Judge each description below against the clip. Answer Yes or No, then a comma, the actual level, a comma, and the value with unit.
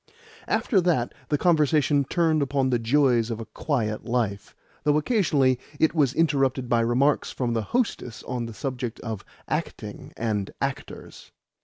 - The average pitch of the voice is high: No, low, 130 Hz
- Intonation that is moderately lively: Yes, average, 4.2 semitones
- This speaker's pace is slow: No, average, 150 wpm